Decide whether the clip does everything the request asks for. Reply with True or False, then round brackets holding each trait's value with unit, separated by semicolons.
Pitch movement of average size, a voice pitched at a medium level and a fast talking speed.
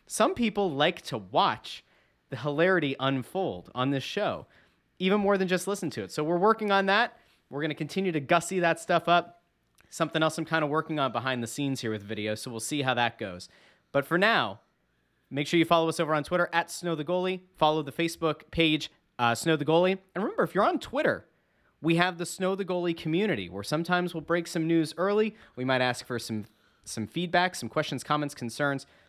True (4.5 semitones; 160 Hz; 220 wpm)